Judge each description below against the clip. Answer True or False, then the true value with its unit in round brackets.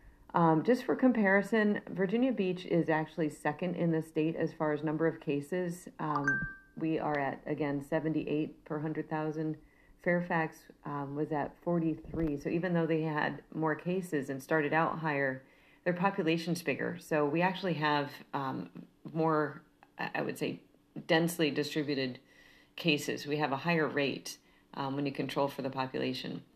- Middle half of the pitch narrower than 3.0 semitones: True (2.5 semitones)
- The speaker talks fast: False (155 wpm)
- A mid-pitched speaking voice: True (155 Hz)